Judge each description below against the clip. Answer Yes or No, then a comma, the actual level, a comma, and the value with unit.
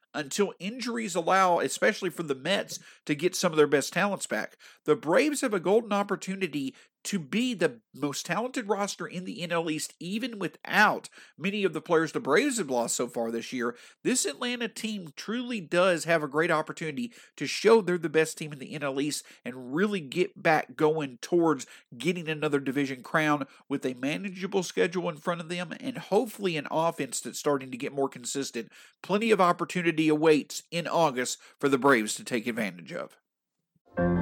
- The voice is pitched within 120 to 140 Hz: No, medium, 170 Hz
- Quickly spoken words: No, average, 185 wpm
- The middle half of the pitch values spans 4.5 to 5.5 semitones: Yes, average, 4.9 semitones